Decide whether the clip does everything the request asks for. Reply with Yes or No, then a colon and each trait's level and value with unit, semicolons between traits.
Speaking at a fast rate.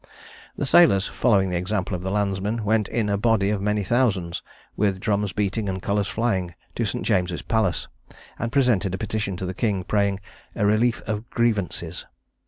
No: average, 180 wpm